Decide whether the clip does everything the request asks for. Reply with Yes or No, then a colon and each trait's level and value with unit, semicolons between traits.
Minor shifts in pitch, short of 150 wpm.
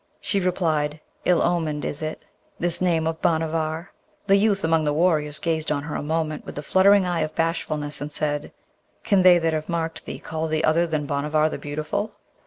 No: narrow, 2.2 semitones; average, 195 wpm